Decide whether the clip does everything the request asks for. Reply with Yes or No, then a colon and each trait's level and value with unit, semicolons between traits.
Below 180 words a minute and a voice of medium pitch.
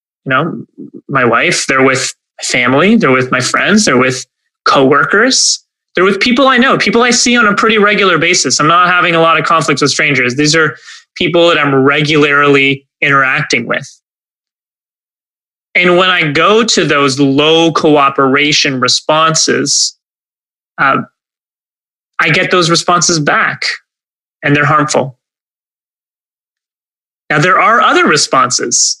Yes: average, 140 wpm; medium, 155 Hz